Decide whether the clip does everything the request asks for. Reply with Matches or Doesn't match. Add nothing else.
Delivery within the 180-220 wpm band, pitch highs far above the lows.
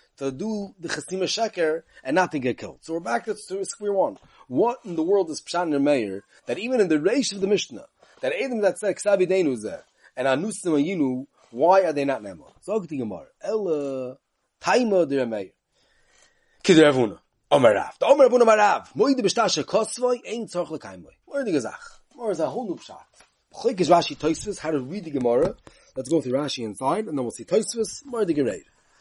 Matches